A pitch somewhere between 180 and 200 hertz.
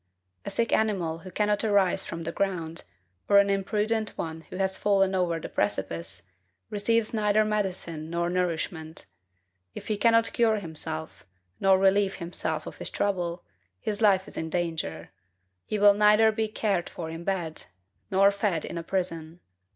Yes: high, 190 Hz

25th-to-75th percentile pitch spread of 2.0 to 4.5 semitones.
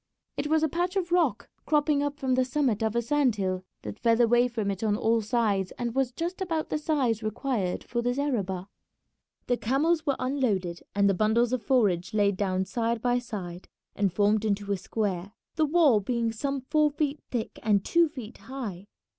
No: wide, 5.6 semitones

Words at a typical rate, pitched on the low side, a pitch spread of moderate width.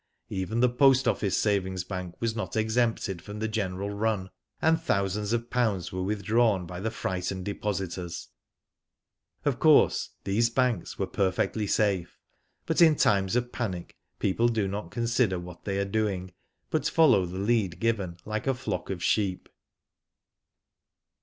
Yes: average, 155 wpm; low, 100 Hz; average, 3.6 semitones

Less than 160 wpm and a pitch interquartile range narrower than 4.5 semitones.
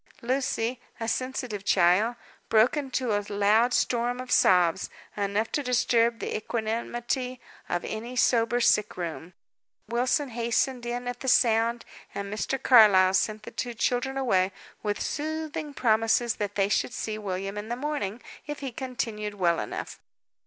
Yes: average, 150 wpm; average, 3.3 semitones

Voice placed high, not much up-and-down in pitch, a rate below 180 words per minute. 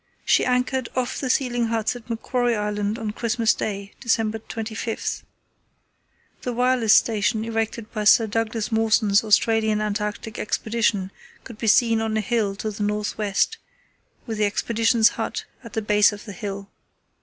Yes: high, 220 Hz; narrow, 1.8 semitones; average, 155 wpm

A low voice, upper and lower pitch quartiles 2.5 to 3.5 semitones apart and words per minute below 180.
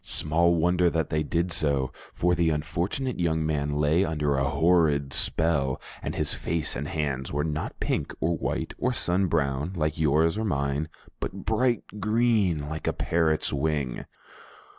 Yes: very low, 80 Hz; average, 3.0 semitones; average, 160 wpm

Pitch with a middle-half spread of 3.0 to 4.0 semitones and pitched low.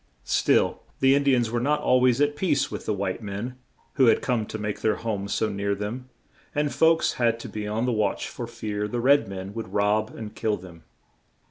Yes: average, 3.7 semitones; low, 110 Hz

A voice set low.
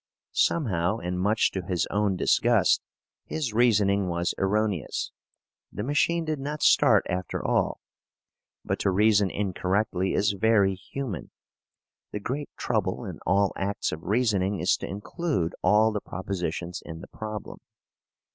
Yes: low, 100 Hz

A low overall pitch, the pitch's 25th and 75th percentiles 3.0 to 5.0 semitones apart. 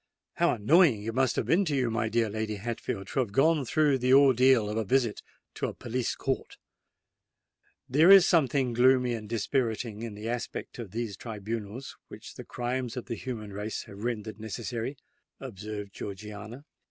Yes: low, 115 Hz; average, 3.4 semitones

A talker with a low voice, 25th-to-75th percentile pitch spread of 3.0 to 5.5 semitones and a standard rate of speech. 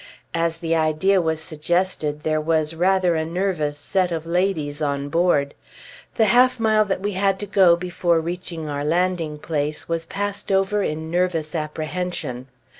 No: medium, 165 Hz; average, 3.3 semitones; average, 160 wpm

